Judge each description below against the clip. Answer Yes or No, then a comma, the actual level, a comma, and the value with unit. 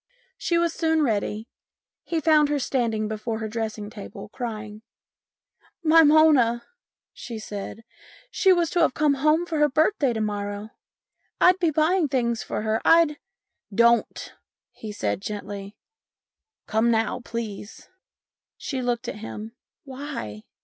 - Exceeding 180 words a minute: No, average, 165 wpm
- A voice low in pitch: No, high, 235 Hz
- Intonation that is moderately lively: No, wide, 6.3 semitones